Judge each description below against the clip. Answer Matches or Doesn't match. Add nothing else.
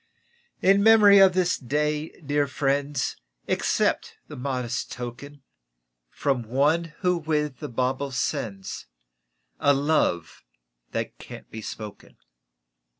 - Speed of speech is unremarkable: Doesn't match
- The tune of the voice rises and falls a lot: Doesn't match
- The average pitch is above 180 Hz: Doesn't match